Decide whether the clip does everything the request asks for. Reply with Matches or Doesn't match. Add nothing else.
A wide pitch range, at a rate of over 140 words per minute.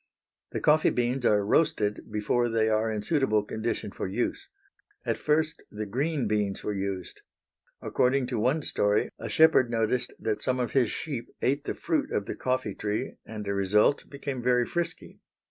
Doesn't match